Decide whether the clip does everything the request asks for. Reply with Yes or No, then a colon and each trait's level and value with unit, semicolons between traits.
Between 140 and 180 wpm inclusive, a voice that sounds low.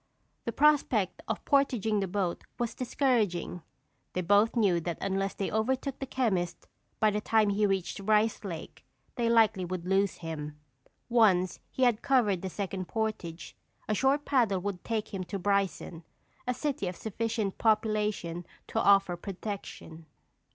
No: average, 150 wpm; high, 205 Hz